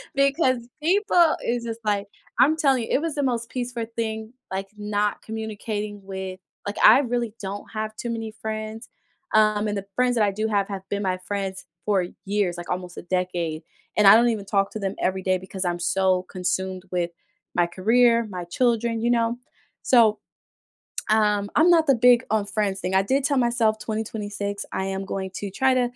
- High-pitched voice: Yes, high, 215 Hz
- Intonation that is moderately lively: Yes, average, 3.5 semitones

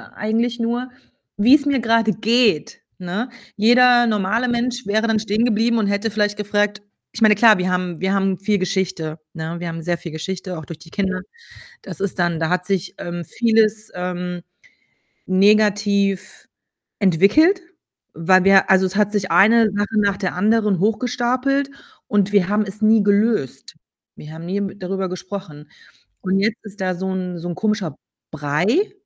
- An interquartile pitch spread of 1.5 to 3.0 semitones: No, average, 3.4 semitones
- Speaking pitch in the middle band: No, high, 200 Hz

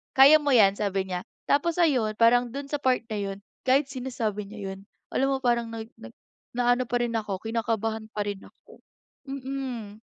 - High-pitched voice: Yes, high, 230 Hz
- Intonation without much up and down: No, average, 4.0 semitones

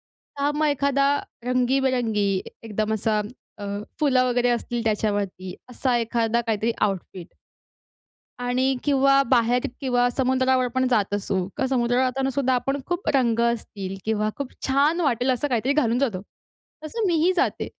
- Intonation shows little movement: No, average, 3.2 semitones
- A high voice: Yes, very high, 250 Hz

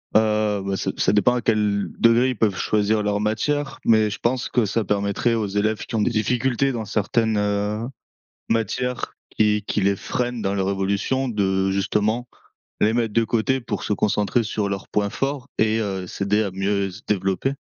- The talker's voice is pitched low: Yes, low, 105 Hz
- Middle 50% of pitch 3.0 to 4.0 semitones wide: No, narrow, 2.5 semitones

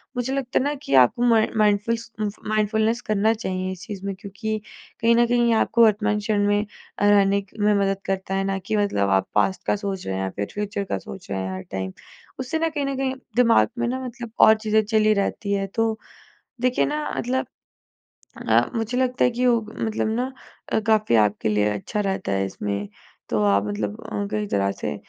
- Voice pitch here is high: Yes, high, 210 Hz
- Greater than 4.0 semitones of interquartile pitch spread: No, average, 3.7 semitones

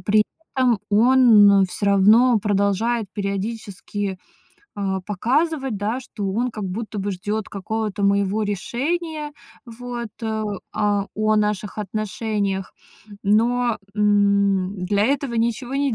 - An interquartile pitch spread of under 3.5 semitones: Yes, average, 2.9 semitones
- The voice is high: Yes, high, 210 Hz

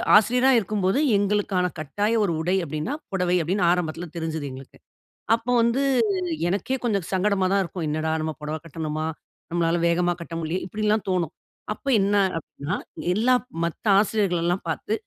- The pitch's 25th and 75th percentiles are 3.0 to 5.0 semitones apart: Yes, average, 4.2 semitones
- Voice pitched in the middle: Yes, medium, 180 Hz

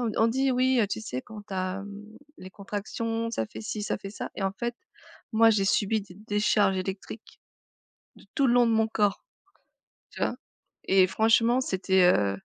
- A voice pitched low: No, high, 210 Hz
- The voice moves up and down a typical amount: Yes, average, 3.0 semitones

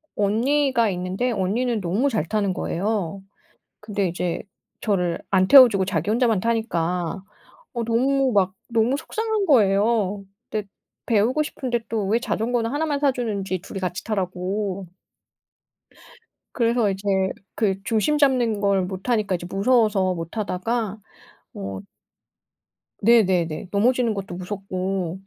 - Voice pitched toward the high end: Yes, high, 210 Hz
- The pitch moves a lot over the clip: No, average, 4.1 semitones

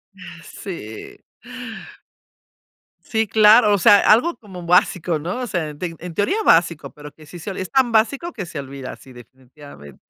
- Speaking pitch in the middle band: Yes, medium, 175 Hz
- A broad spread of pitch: Yes, wide, 6.2 semitones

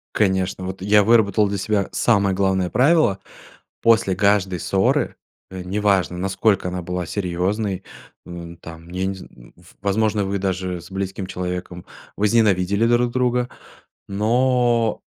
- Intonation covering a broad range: No, average, 2.7 semitones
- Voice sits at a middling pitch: No, low, 100 Hz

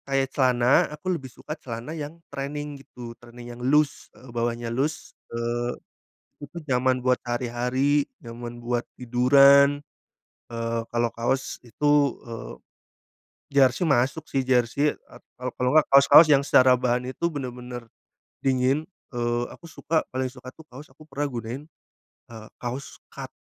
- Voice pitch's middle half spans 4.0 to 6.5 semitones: No, average, 2.7 semitones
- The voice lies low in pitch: Yes, low, 130 Hz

